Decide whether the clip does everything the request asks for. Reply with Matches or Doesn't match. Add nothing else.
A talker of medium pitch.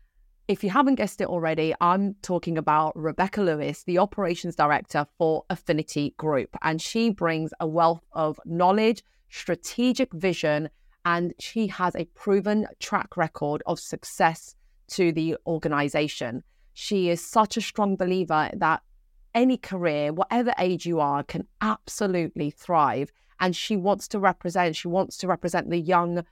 Matches